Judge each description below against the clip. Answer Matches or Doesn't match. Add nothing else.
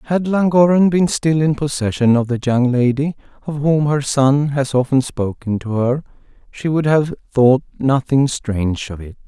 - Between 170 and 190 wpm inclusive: Matches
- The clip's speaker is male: Matches